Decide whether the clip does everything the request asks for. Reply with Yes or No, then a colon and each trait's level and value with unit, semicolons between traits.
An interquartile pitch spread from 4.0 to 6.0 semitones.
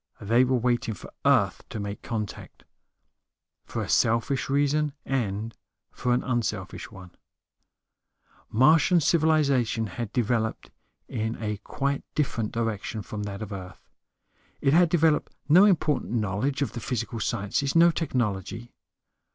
Yes: average, 4.8 semitones